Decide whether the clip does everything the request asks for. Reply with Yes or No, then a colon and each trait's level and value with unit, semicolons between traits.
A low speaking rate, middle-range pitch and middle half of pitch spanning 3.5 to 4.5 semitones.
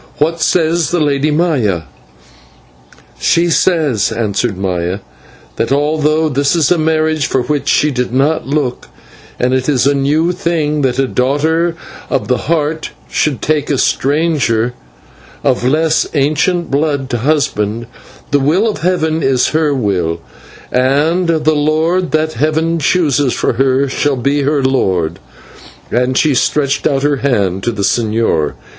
No: average, 150 wpm; medium, 145 Hz; average, 3.9 semitones